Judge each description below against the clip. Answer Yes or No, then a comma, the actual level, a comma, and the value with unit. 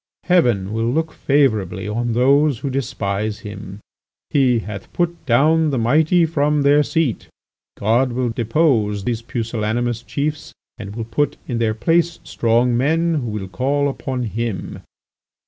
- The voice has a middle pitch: No, low, 120 Hz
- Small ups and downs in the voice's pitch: No, average, 4.8 semitones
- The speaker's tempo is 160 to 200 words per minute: No, average, 145 wpm